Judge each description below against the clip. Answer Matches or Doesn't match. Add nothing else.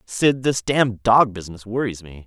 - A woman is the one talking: Doesn't match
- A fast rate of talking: Doesn't match